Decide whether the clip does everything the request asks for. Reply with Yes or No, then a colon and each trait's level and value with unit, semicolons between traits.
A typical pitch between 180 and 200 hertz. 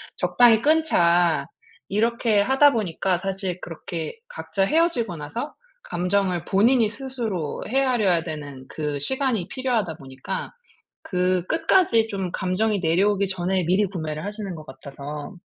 Yes: high, 195 Hz